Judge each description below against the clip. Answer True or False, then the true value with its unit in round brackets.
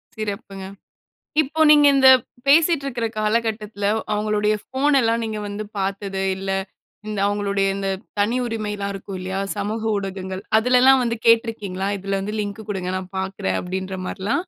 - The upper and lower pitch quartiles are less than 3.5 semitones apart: True (2.8 semitones)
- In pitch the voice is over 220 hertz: False (205 Hz)